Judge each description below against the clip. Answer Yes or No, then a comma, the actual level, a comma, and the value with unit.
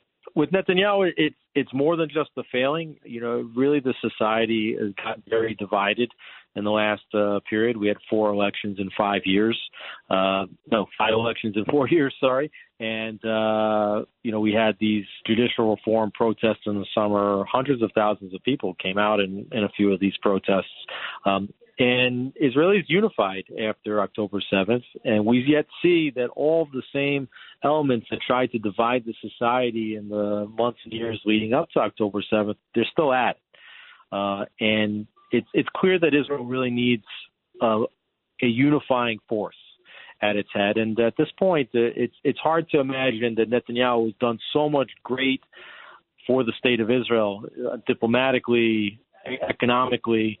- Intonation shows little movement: No, average, 3.4 semitones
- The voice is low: Yes, low, 115 Hz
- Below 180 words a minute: Yes, average, 170 wpm